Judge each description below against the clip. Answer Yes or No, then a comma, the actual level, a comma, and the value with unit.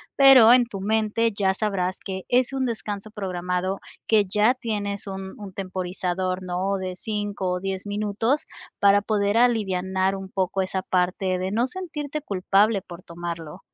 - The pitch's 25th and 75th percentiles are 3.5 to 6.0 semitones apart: No, average, 2.7 semitones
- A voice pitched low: No, high, 195 Hz